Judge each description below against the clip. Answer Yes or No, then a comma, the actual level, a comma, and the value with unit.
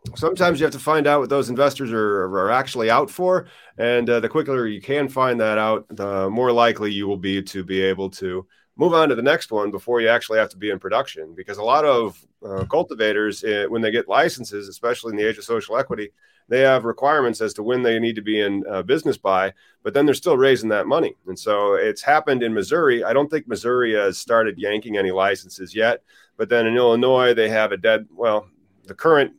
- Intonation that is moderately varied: Yes, average, 4.7 semitones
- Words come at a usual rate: No, fast, 230 wpm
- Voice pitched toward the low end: Yes, low, 115 Hz